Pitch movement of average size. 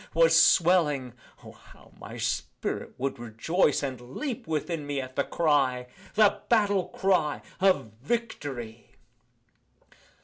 No: wide, 6.1 semitones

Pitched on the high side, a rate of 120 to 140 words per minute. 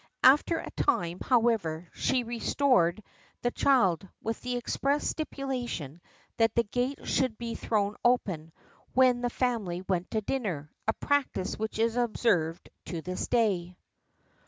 Yes: high, 225 Hz; slow, 135 wpm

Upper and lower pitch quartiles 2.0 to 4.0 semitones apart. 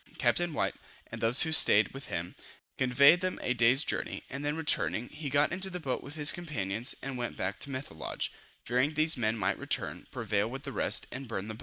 No: average, 5.0 semitones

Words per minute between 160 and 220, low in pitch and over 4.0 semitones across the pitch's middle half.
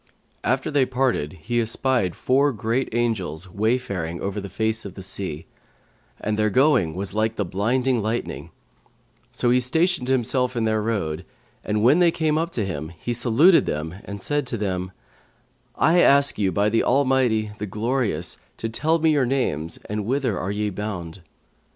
Yes: average, 170 wpm; low, 110 Hz; average, 4.9 semitones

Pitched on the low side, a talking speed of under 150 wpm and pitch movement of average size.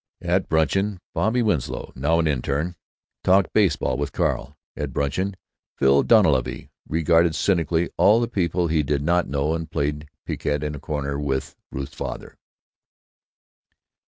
Yes: very low, 80 Hz; average, 140 wpm; average, 3.8 semitones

